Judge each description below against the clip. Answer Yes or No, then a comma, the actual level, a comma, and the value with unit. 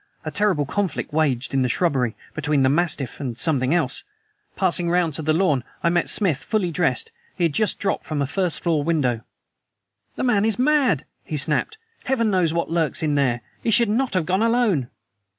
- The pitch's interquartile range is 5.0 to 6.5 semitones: Yes, wide, 5.6 semitones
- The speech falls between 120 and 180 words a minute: No, average, 190 wpm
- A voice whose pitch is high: No, medium, 165 Hz